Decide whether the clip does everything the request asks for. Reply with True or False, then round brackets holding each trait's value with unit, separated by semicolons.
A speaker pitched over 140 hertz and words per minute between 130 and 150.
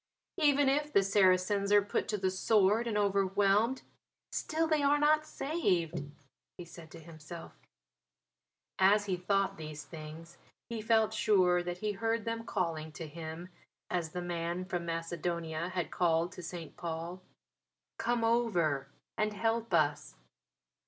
True (185 Hz; 145 wpm)